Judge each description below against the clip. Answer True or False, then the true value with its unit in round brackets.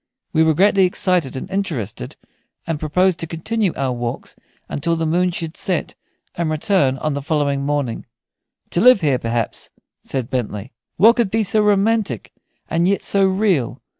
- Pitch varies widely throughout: True (5.8 semitones)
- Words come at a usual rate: True (165 wpm)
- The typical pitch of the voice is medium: True (165 Hz)